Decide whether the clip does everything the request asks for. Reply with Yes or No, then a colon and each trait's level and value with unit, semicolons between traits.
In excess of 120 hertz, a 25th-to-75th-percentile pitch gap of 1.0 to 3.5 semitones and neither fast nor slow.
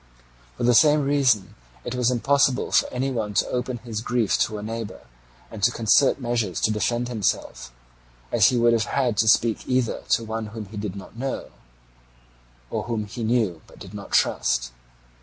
No: low, 115 Hz; narrow, 2.6 semitones; average, 185 wpm